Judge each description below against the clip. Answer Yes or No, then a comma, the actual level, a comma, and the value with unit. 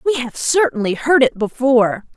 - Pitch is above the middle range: Yes, very high, 255 Hz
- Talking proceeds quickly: No, average, 165 wpm